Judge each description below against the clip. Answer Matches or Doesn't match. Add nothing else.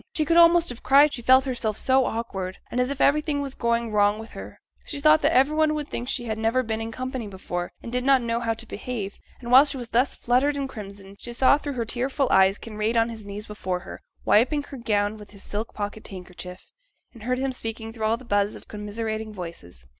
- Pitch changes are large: Doesn't match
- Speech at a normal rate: Doesn't match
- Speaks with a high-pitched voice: Matches